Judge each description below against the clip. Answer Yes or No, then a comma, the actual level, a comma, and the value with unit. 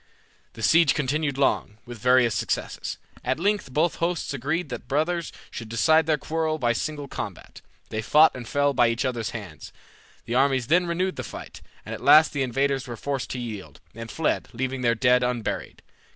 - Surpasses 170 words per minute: Yes, average, 190 wpm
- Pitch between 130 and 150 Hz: Yes, low, 135 Hz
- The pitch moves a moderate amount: Yes, average, 4.5 semitones